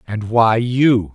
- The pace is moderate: Yes, average, 155 wpm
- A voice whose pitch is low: Yes, low, 115 Hz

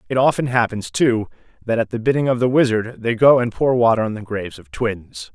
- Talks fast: Yes, fast, 235 wpm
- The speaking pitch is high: No, low, 115 Hz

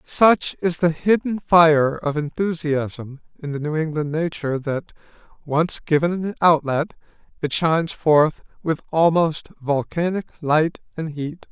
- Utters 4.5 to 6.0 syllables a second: No, 4.1 syllables/s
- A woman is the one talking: No, male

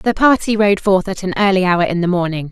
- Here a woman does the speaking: Yes, female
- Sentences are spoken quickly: Yes, fast, 260 wpm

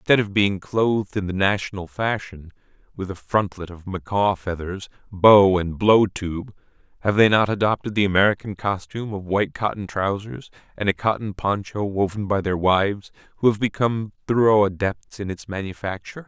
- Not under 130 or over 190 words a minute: Yes, average, 165 wpm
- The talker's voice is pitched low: Yes, low, 100 Hz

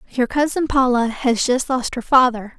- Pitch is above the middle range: Yes, very high, 250 Hz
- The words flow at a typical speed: Yes, average, 185 wpm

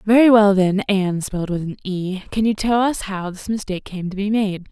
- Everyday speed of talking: No, fast, 240 wpm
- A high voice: Yes, high, 200 Hz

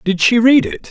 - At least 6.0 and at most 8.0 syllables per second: No, 4.9 syllables/s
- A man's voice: Yes, male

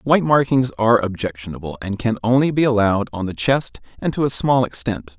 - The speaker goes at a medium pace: Yes, average, 195 wpm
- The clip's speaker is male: Yes, male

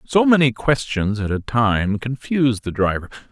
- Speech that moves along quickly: No, average, 165 wpm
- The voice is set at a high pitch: No, low, 120 Hz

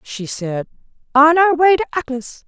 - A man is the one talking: No, female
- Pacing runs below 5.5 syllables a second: Yes, 4.5 syllables/s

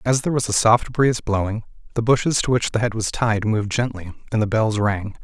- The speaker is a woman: No, male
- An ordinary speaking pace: No, fast, 240 wpm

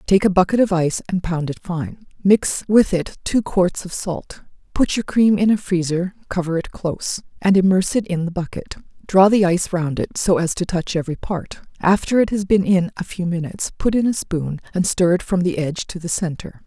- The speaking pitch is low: No, medium, 185 Hz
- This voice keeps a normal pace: No, fast, 225 wpm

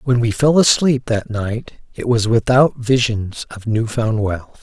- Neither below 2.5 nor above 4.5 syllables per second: Yes, 4.0 syllables/s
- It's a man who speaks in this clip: Yes, male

